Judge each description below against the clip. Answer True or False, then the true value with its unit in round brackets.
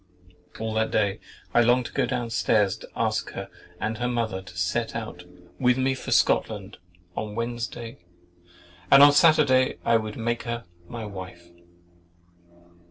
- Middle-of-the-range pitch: False (115 Hz)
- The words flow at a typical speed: True (160 wpm)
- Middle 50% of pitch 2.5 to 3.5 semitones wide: True (2.8 semitones)